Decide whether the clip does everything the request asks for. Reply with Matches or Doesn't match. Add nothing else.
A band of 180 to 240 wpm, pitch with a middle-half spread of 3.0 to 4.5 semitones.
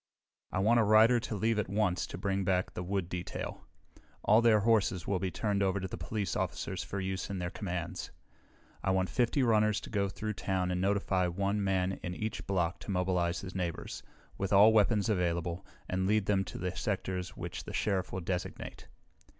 Doesn't match